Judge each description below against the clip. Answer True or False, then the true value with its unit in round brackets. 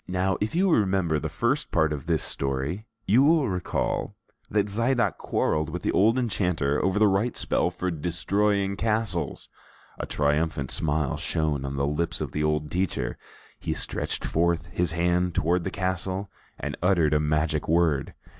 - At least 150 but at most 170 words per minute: True (165 wpm)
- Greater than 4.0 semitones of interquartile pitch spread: True (4.6 semitones)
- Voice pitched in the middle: False (90 Hz)